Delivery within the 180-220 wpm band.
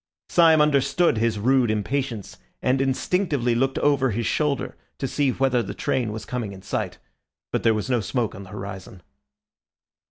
No: average, 165 wpm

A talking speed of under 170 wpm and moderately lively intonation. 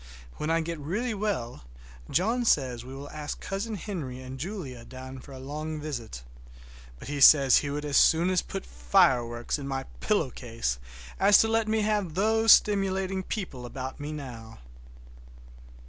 No: average, 160 wpm; wide, 7.2 semitones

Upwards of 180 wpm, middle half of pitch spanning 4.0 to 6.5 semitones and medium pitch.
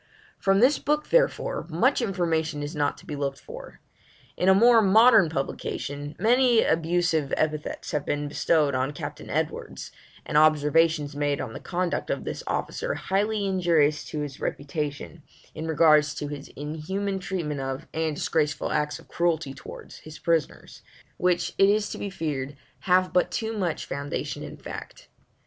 No: average, 160 wpm; average, 4.7 semitones; medium, 160 Hz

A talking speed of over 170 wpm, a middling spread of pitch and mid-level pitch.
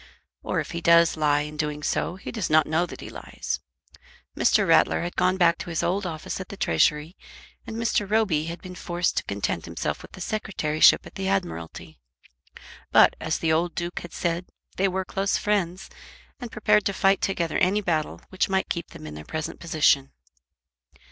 Yes: average, 195 wpm; average, 3.5 semitones; medium, 175 Hz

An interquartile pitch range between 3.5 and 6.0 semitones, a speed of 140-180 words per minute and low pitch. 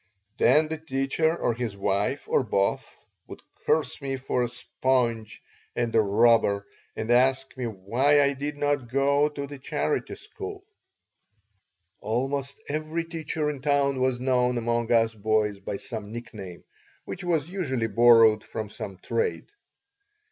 Yes: average, 4.1 semitones; average, 145 wpm; low, 130 Hz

